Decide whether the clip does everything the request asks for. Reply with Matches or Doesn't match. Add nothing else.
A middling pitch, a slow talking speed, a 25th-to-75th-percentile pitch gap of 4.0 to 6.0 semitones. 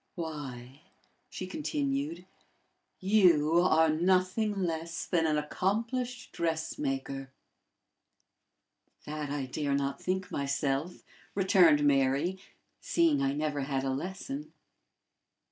Matches